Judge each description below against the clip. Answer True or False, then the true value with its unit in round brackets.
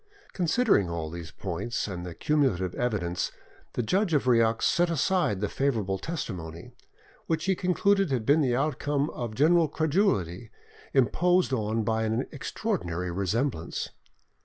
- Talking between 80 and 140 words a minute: True (135 wpm)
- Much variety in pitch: True (8.8 semitones)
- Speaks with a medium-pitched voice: False (120 Hz)